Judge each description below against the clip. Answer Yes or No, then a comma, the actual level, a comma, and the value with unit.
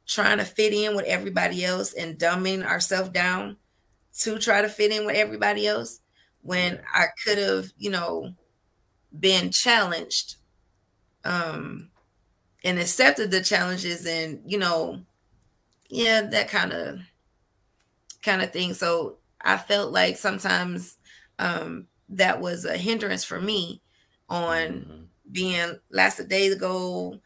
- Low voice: No, medium, 175 Hz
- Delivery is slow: Yes, slow, 130 wpm